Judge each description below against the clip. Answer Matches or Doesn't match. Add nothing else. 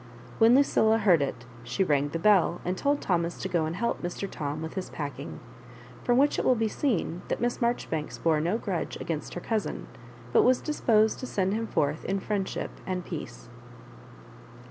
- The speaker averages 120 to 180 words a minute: Doesn't match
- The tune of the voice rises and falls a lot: Matches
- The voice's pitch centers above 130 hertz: Matches